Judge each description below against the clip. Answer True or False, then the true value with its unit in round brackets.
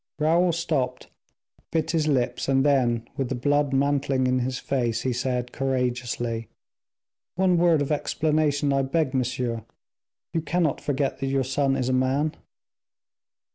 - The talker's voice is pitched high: False (135 Hz)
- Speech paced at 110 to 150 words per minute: True (145 wpm)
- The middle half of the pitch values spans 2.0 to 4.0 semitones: True (2.8 semitones)